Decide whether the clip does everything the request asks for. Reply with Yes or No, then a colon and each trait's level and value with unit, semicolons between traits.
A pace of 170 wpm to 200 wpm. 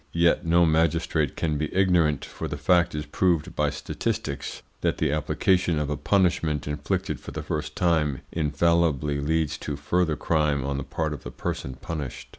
Yes: average, 175 wpm